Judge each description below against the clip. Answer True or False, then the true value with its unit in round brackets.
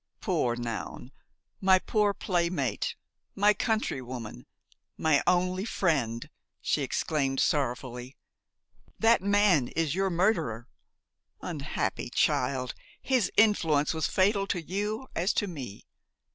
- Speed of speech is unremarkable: False (105 wpm)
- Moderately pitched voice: True (165 Hz)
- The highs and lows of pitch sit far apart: True (7.4 semitones)